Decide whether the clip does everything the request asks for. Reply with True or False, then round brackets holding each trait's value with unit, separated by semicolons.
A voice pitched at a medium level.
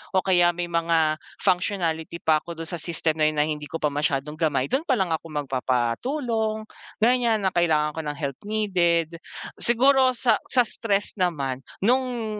True (170 Hz)